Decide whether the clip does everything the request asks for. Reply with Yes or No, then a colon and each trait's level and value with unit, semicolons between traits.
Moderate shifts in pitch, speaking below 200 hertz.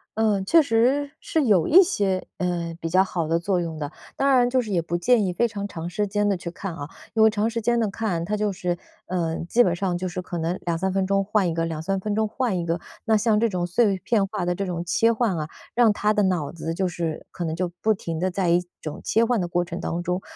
Yes: average, 3.9 semitones; high, 190 Hz